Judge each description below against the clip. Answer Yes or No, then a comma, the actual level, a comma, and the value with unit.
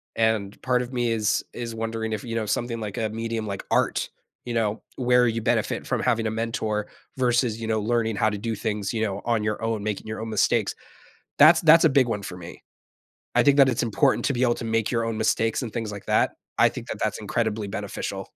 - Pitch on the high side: No, low, 115 Hz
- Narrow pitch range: Yes, narrow, 1.9 semitones